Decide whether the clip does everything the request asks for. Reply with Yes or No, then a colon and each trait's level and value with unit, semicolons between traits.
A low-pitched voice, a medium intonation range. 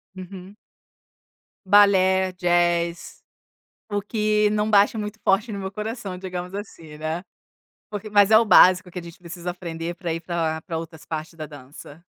No: medium, 185 Hz; average, 3.3 semitones